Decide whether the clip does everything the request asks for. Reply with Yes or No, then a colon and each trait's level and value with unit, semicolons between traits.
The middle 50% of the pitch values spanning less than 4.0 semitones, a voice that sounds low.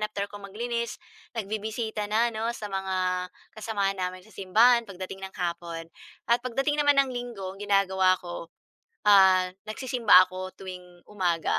No: average, 3.5 semitones; high, 200 Hz